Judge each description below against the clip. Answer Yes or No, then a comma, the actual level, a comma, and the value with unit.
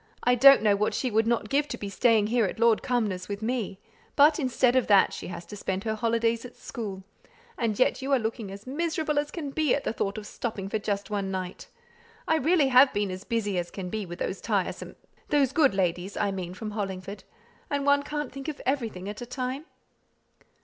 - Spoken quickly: Yes, fast, 220 wpm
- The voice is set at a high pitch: Yes, high, 225 Hz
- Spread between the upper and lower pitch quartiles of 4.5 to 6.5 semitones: Yes, average, 5.1 semitones